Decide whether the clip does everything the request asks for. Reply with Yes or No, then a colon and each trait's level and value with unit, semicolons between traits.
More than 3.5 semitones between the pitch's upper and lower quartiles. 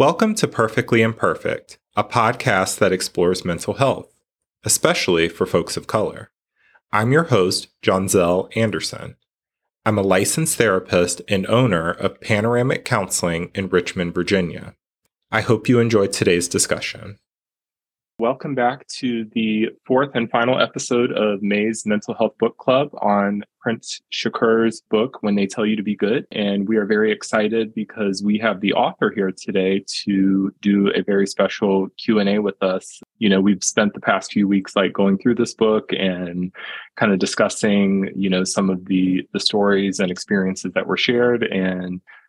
No: average, 2.9 semitones